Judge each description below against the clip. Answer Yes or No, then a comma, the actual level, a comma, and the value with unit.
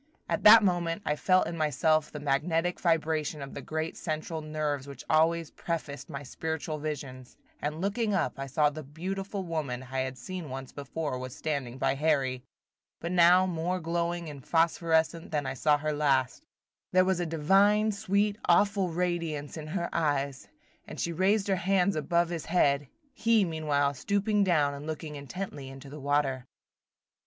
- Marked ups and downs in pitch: No, average, 3.8 semitones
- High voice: No, medium, 160 Hz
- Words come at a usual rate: Yes, average, 170 wpm